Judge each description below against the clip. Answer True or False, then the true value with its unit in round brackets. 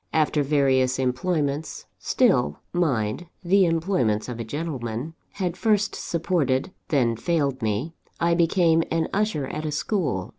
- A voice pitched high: False (150 Hz)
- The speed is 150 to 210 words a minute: False (135 wpm)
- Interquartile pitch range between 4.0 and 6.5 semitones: True (4.8 semitones)